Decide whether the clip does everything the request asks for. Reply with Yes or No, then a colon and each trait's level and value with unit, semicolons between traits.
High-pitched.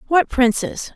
Yes: very high, 280 Hz